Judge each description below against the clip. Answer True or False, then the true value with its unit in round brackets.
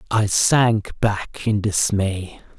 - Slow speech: True (115 wpm)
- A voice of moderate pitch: False (105 Hz)